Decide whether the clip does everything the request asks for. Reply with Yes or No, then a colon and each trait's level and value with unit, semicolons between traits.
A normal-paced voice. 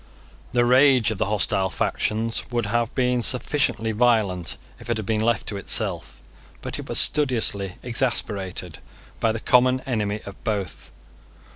Yes: average, 150 wpm